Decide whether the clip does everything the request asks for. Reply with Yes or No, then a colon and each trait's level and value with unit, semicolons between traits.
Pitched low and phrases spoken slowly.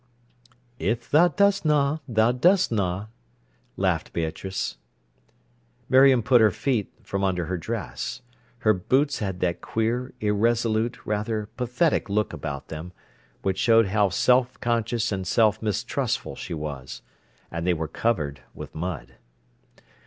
Yes: low, 110 Hz; slow, 125 wpm